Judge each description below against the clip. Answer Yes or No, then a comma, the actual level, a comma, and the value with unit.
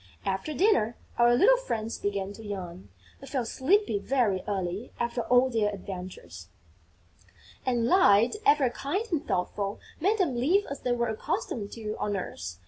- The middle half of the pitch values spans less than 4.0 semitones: No, wide, 5.4 semitones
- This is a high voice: Yes, high, 230 Hz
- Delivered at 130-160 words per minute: Yes, average, 155 wpm